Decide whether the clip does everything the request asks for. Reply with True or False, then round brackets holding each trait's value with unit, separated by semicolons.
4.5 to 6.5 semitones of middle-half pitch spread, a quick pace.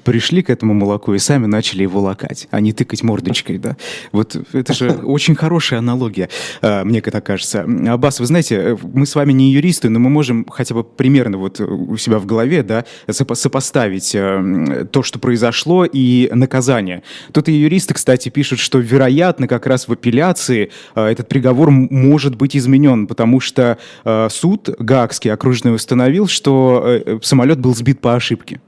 False (3.7 semitones; 165 wpm)